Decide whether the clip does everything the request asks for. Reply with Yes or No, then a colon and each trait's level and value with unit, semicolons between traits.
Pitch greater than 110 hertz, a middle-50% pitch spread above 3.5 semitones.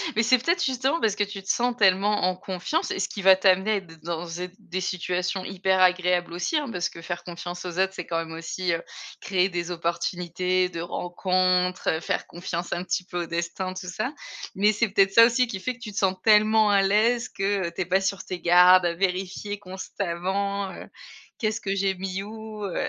No: high, 190 Hz; narrow, 2.4 semitones